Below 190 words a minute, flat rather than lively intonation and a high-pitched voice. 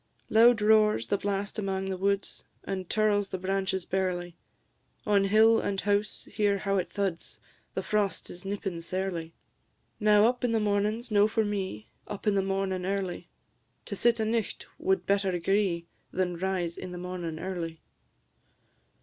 Yes: average, 160 wpm; narrow, 2.2 semitones; high, 195 Hz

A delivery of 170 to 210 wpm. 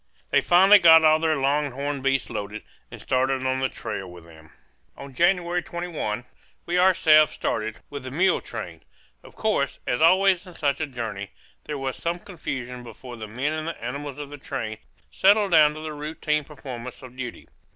Yes: average, 180 wpm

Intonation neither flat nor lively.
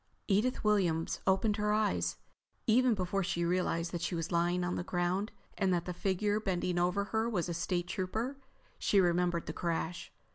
Yes: average, 3.0 semitones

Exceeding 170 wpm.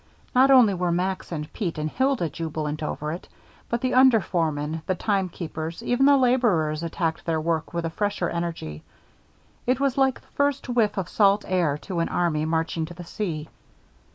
Yes: average, 180 wpm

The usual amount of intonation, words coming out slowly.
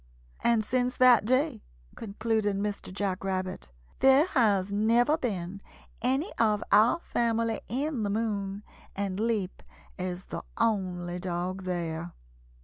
Yes: average, 4.0 semitones; slow, 130 wpm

